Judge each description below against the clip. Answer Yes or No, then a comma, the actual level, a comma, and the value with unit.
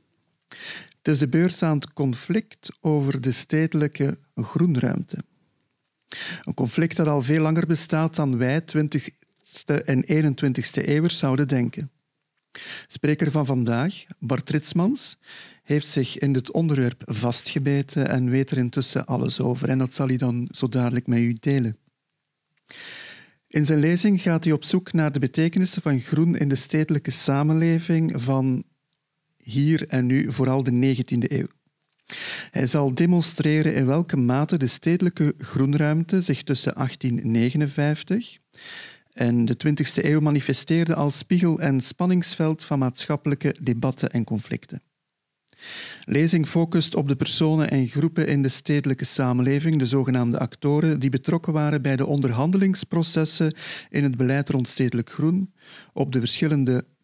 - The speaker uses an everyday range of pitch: Yes, average, 3.3 semitones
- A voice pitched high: No, medium, 145 Hz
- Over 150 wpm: No, average, 140 wpm